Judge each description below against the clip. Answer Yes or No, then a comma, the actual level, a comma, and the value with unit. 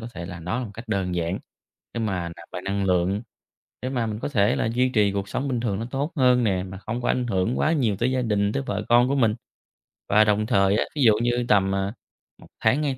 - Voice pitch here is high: No, low, 110 Hz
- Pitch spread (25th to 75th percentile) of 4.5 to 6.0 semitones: No, average, 4.0 semitones